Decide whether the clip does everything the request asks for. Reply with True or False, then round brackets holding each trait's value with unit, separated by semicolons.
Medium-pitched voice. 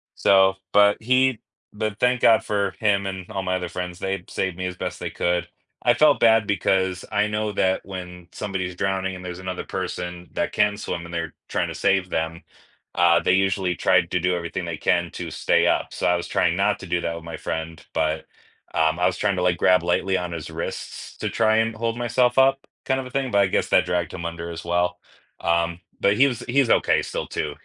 False (95 Hz)